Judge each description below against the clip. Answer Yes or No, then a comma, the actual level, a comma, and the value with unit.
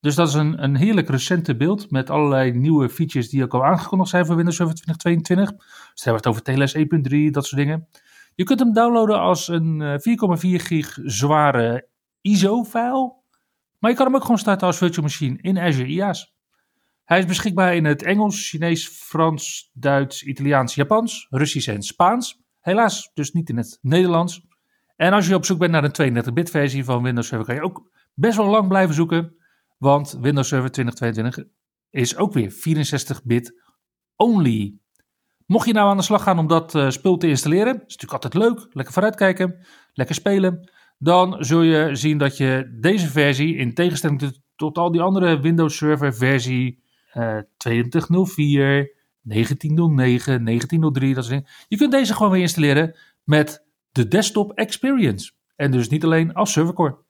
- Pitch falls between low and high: Yes, medium, 160 Hz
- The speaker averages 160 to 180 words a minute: Yes, average, 170 wpm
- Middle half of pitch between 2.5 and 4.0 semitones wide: No, average, 5.2 semitones